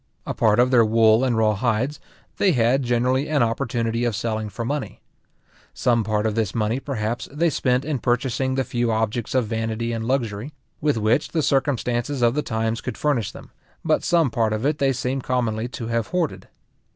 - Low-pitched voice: Yes, low, 120 Hz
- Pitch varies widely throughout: No, average, 3.2 semitones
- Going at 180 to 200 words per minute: Yes, average, 195 wpm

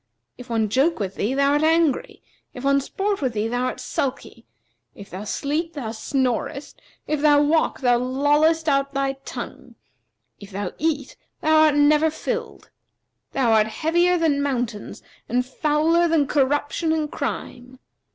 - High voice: Yes, very high, 280 Hz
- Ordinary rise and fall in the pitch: Yes, average, 3.9 semitones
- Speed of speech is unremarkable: Yes, average, 155 wpm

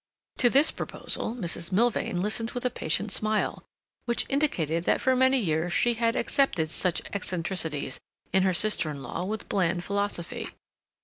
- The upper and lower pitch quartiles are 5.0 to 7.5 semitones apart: Yes, wide, 5.6 semitones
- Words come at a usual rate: Yes, average, 160 wpm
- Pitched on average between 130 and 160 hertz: No, high, 200 Hz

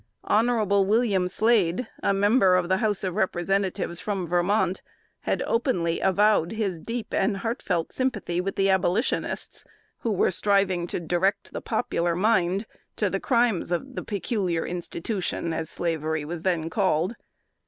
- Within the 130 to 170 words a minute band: Yes, average, 150 wpm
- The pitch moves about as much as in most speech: Yes, average, 3.6 semitones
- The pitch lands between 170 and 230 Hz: Yes, high, 190 Hz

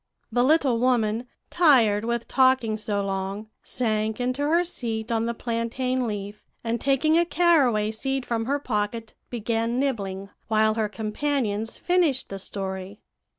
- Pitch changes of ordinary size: Yes, average, 3.5 semitones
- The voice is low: No, high, 230 Hz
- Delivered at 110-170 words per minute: Yes, average, 145 wpm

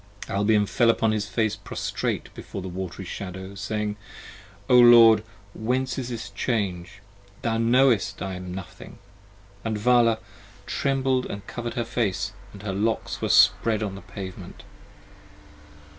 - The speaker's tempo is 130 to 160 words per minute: Yes, average, 145 wpm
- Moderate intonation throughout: Yes, average, 3.2 semitones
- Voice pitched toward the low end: Yes, low, 105 Hz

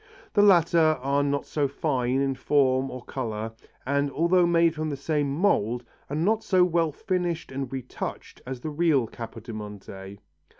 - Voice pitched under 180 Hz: Yes, medium, 140 Hz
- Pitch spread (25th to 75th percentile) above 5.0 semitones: No, average, 4.5 semitones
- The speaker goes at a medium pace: Yes, average, 160 wpm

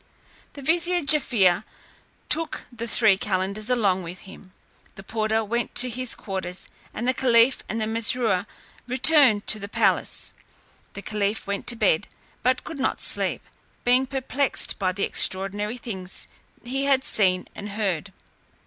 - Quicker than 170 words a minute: No, average, 145 wpm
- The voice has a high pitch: Yes, high, 220 Hz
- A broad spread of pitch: No, average, 4.4 semitones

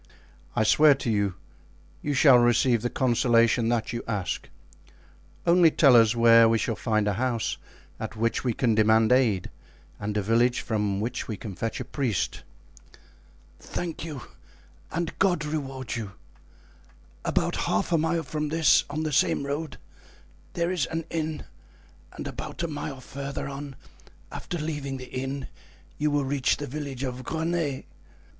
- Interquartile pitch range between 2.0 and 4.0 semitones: No, average, 4.8 semitones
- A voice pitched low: Yes, low, 130 Hz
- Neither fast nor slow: Yes, average, 155 wpm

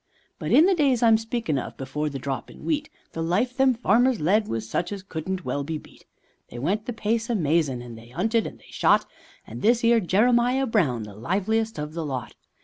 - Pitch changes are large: Yes, wide, 8.0 semitones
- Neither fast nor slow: No, fast, 210 wpm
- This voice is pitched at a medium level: No, high, 195 Hz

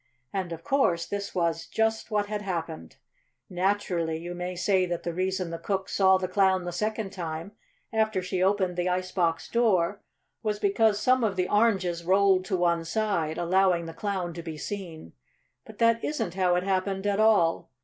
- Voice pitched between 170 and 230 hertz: Yes, medium, 185 Hz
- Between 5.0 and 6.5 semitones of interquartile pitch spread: No, average, 2.9 semitones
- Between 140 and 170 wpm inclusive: No, average, 185 wpm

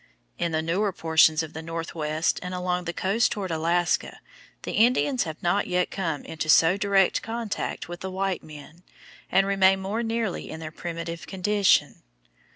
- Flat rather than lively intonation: No, average, 3.3 semitones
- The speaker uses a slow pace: No, average, 165 wpm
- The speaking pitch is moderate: Yes, medium, 180 Hz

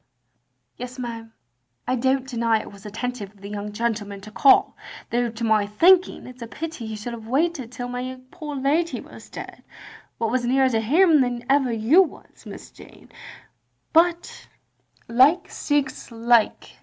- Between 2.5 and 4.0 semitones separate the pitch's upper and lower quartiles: Yes, average, 3.3 semitones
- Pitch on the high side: Yes, high, 245 Hz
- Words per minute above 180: No, average, 175 wpm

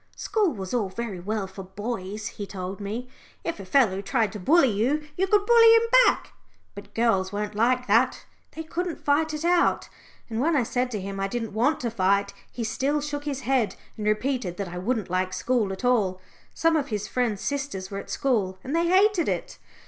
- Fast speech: Yes, fast, 210 wpm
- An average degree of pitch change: No, wide, 6.3 semitones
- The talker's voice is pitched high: Yes, high, 230 Hz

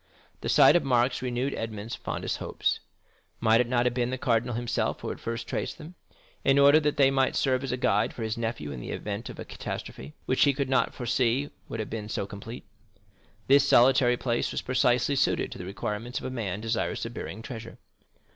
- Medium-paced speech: No, fast, 210 wpm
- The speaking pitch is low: Yes, low, 120 Hz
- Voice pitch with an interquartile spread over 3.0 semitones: No, narrow, 2.6 semitones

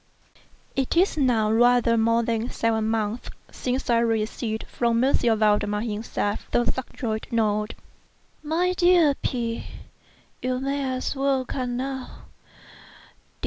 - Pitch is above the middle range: Yes, high, 235 Hz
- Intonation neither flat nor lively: Yes, average, 3.0 semitones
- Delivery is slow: Yes, slow, 120 wpm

